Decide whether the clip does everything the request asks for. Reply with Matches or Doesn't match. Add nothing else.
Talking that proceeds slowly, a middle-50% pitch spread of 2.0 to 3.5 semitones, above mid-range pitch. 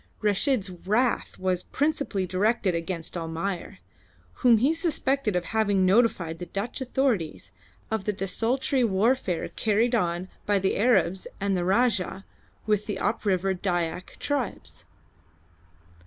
Doesn't match